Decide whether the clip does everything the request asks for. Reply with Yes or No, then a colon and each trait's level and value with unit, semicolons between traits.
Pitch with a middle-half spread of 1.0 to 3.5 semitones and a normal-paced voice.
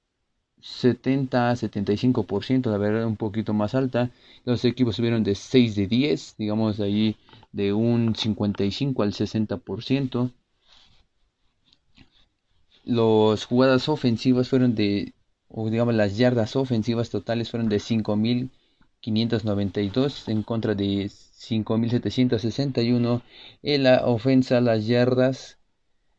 No: average, 2.8 semitones; slow, 110 wpm